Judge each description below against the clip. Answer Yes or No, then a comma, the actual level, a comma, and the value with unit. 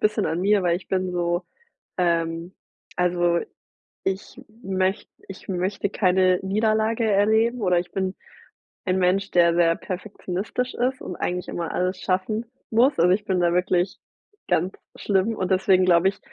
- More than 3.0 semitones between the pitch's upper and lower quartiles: No, narrow, 2.4 semitones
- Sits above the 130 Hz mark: Yes, medium, 185 Hz